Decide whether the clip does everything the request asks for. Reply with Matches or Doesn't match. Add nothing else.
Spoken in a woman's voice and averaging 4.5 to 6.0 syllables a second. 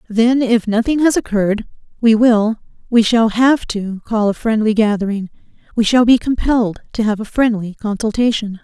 Matches